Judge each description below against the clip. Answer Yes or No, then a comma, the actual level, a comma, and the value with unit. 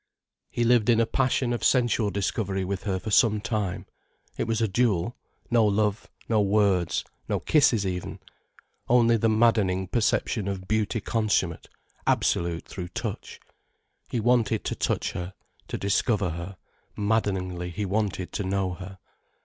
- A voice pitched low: Yes, low, 105 Hz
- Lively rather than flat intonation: No, average, 3.3 semitones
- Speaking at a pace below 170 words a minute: Yes, average, 145 wpm